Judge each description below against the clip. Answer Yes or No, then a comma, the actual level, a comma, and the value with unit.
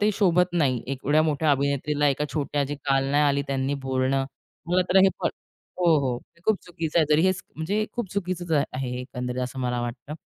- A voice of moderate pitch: Yes, medium, 145 Hz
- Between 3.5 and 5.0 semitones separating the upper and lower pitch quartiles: Yes, average, 4.5 semitones